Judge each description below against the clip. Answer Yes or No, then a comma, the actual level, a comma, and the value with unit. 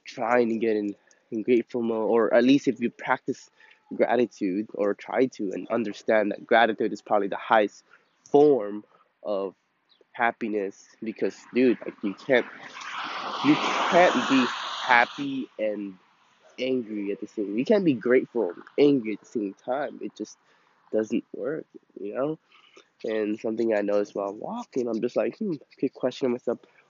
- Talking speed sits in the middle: Yes, average, 160 wpm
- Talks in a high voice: No, low, 115 Hz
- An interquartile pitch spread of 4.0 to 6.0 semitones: Yes, average, 4.6 semitones